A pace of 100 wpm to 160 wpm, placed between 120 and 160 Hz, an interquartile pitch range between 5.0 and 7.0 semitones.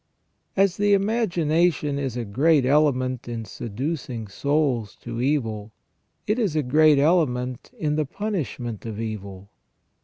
Yes: slow, 135 wpm; medium, 140 Hz; wide, 5.4 semitones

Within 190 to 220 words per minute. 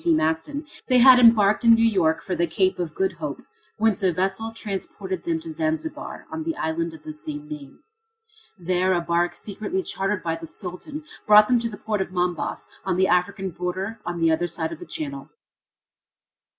Yes: average, 195 wpm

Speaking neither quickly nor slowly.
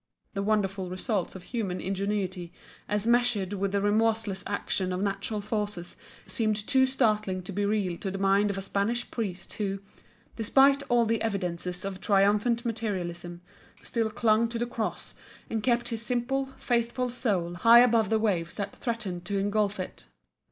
Yes: average, 165 wpm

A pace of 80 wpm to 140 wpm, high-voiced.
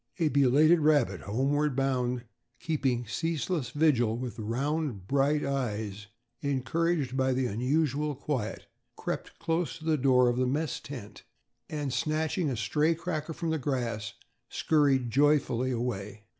No: slow, 135 wpm; low, 135 Hz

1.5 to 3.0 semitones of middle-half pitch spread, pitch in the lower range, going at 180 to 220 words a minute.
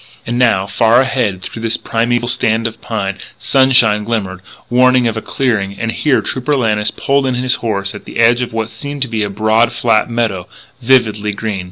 Yes: average, 2.7 semitones; low, 115 Hz; average, 195 wpm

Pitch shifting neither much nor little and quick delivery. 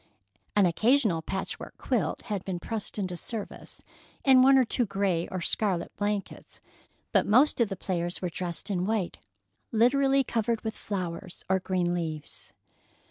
No: average, 4.2 semitones; average, 150 wpm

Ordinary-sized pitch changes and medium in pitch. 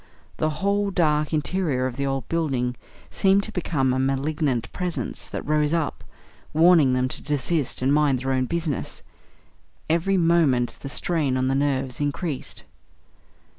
Yes: average, 4.1 semitones; medium, 145 Hz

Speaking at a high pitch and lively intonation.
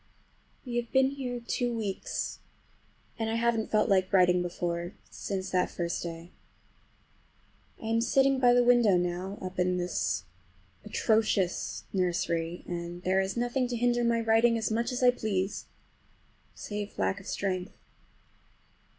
No: high, 205 Hz; average, 4.7 semitones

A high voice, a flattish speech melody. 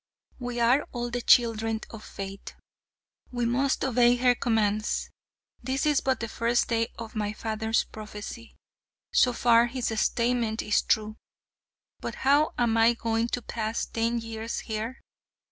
Yes: high, 230 Hz; narrow, 1.6 semitones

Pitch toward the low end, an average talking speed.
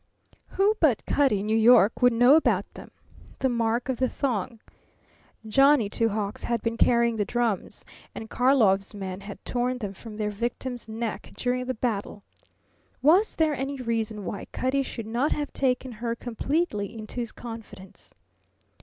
No: high, 235 Hz; average, 165 wpm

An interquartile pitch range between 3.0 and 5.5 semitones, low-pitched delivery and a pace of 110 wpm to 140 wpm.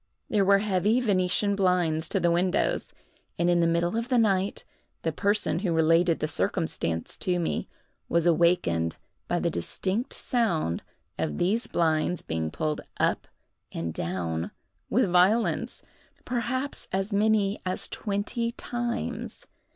No: average, 4.5 semitones; medium, 180 Hz; slow, 135 wpm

